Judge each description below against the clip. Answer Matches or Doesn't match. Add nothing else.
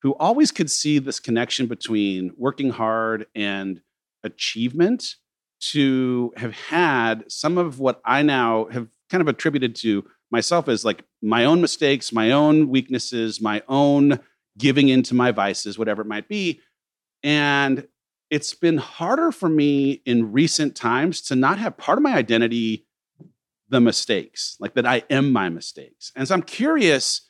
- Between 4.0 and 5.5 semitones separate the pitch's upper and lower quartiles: Matches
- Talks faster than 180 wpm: Doesn't match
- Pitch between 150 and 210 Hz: Doesn't match